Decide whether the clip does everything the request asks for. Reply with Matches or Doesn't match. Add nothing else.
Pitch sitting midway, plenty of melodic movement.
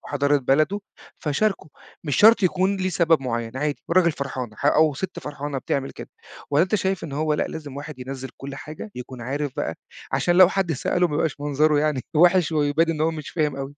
Doesn't match